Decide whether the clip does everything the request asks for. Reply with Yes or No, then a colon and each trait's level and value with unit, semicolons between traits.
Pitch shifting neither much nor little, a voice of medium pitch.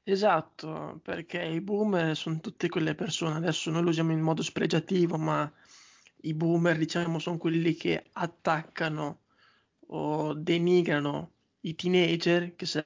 No: narrow, 1.6 semitones; medium, 165 Hz